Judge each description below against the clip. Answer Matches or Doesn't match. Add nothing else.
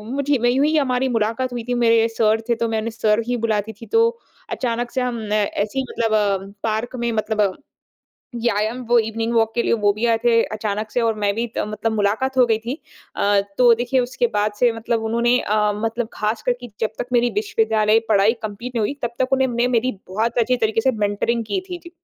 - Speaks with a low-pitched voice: Doesn't match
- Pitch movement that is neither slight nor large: Doesn't match